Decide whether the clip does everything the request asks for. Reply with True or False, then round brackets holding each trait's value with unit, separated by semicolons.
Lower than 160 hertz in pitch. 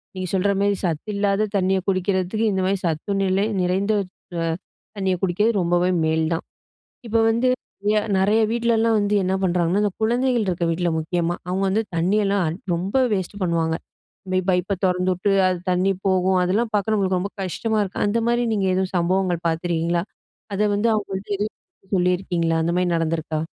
False (190 Hz)